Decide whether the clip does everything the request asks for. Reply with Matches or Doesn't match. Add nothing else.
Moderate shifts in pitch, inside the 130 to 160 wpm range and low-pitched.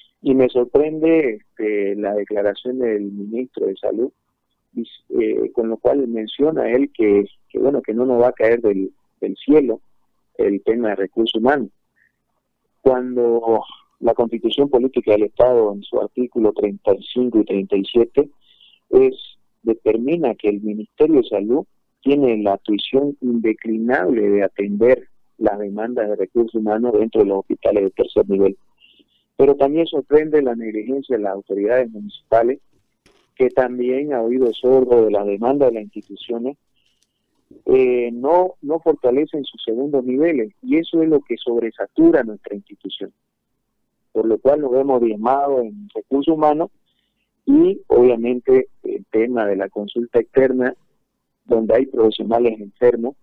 Matches